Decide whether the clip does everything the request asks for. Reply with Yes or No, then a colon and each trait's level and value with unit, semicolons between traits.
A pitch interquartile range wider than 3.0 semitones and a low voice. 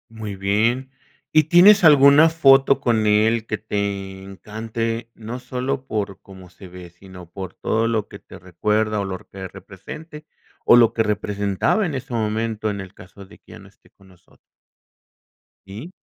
Yes: average, 4.2 semitones; low, 110 Hz